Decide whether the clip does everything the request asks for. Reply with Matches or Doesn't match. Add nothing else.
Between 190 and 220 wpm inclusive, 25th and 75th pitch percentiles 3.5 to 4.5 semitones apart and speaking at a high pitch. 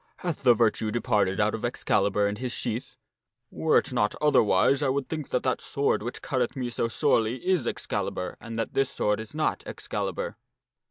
Doesn't match